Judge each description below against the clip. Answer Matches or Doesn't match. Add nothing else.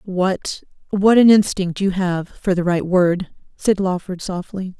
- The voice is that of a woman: Matches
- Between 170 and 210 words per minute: Doesn't match